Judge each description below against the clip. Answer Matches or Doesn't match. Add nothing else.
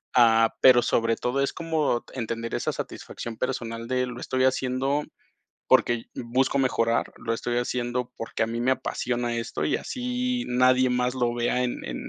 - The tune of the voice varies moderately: Doesn't match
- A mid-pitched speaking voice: Doesn't match